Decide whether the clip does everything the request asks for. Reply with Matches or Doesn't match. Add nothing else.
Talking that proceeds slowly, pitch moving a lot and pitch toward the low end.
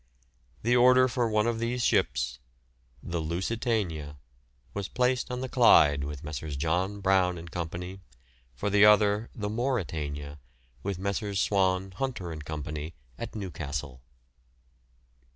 Matches